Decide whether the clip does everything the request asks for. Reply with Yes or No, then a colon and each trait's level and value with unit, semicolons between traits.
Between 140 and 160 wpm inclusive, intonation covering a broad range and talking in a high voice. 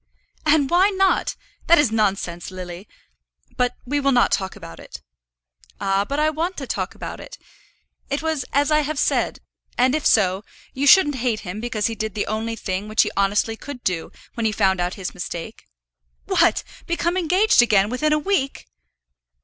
No: average, 180 wpm; wide, 7.2 semitones; high, 240 Hz